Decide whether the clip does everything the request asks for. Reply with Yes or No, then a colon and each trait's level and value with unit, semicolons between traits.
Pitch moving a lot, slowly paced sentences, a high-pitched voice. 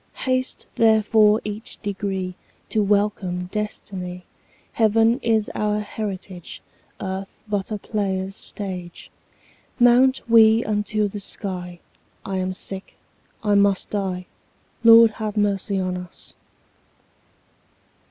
No: narrow, 2.4 semitones; slow, 115 wpm; high, 205 Hz